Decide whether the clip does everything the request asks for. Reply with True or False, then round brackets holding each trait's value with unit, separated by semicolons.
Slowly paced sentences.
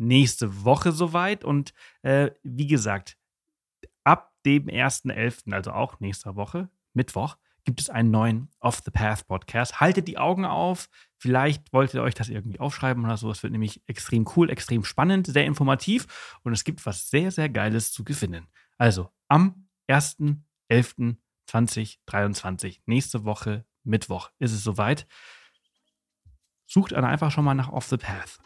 False (140 wpm)